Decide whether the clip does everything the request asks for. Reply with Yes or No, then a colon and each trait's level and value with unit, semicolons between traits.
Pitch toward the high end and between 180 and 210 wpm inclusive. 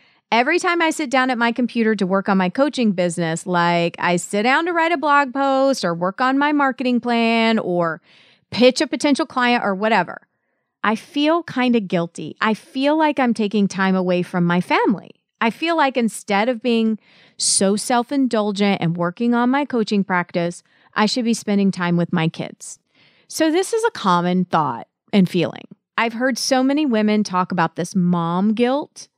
Yes: high, 220 Hz; average, 190 wpm